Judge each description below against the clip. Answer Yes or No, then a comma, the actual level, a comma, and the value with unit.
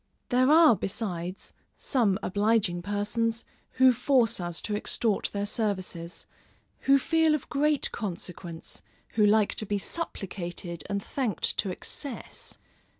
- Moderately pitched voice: No, high, 210 Hz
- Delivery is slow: Yes, slow, 125 wpm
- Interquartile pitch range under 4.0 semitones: No, average, 5.1 semitones